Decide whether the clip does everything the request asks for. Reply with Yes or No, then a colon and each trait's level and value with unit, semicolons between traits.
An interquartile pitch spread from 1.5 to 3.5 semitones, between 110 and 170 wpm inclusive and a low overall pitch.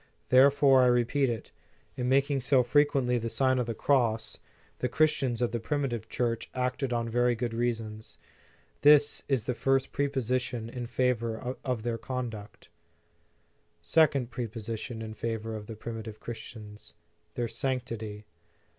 Yes: narrow, 2.6 semitones; average, 145 wpm; low, 120 Hz